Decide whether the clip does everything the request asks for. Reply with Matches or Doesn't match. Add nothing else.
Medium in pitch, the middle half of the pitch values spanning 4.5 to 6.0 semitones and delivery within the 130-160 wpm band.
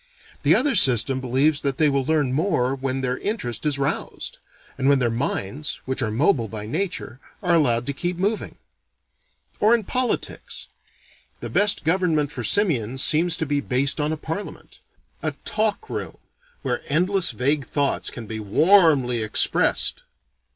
Matches